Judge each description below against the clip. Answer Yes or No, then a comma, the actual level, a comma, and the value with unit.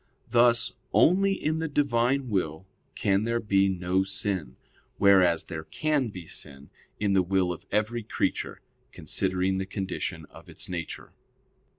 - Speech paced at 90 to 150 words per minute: Yes, average, 145 wpm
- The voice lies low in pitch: Yes, very low, 95 Hz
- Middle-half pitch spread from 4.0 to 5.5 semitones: Yes, average, 4.5 semitones